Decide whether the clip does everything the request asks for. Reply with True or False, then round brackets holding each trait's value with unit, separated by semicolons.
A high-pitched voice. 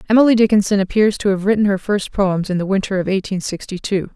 True (200 Hz)